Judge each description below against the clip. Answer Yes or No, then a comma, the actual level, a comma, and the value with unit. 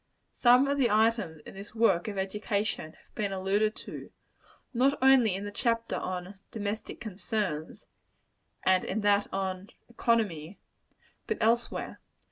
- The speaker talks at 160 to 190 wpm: No, slow, 135 wpm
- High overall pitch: Yes, high, 205 Hz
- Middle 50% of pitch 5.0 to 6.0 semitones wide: No, average, 3.3 semitones